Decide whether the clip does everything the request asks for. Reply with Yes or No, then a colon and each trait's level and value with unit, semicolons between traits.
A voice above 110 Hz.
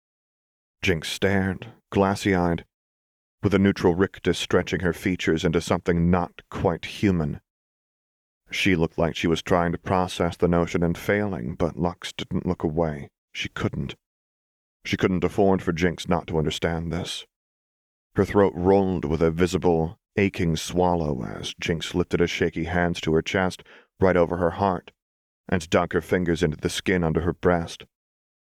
No: very low, 90 Hz